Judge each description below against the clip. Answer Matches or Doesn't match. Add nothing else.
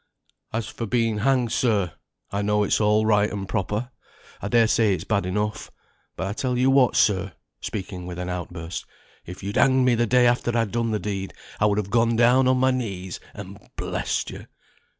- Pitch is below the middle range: Matches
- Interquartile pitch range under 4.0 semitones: Matches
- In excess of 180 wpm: Matches